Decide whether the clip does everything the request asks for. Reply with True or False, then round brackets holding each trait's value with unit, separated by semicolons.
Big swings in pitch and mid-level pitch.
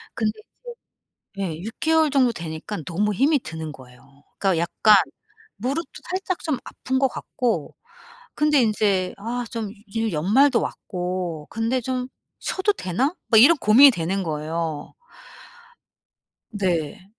False (7.2 semitones; 210 Hz)